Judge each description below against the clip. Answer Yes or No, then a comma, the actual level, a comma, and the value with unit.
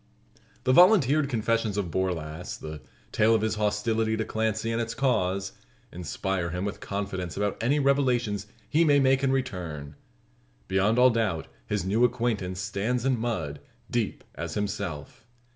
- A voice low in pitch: Yes, low, 110 Hz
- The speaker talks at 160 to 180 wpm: No, average, 150 wpm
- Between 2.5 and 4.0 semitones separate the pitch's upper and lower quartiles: No, average, 4.5 semitones